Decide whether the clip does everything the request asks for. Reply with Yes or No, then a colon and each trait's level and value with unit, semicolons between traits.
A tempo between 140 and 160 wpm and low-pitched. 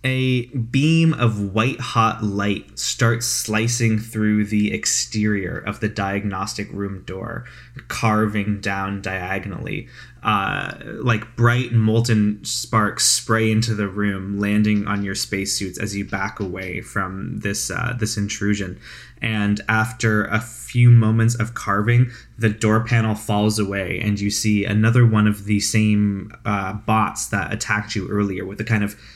Yes: average, 145 wpm; low, 105 Hz